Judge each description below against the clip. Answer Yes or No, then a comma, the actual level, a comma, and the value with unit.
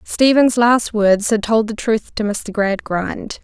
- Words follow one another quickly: No, average, 175 wpm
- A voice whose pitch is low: No, high, 220 Hz